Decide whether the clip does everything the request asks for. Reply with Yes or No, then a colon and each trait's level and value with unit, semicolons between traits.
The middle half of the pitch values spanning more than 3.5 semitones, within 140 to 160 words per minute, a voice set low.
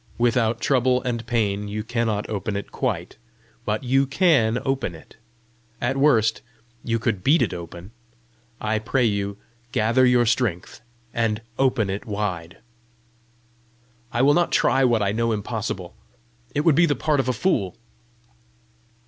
Yes: average, 3.9 semitones; average, 150 wpm; low, 115 Hz